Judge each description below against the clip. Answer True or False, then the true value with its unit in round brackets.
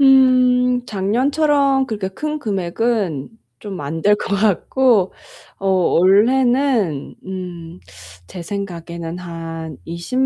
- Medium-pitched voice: False (200 Hz)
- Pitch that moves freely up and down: True (6.6 semitones)